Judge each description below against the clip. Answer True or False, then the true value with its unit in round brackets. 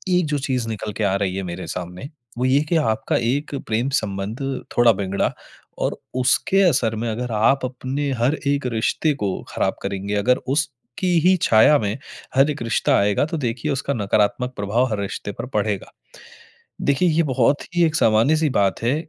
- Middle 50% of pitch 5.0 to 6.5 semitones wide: True (5.3 semitones)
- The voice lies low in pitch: True (120 Hz)